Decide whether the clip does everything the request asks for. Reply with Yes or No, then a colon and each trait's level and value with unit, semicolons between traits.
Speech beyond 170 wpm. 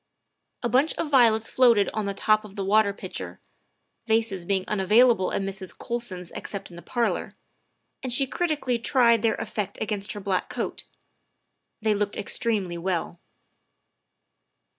No: average, 145 wpm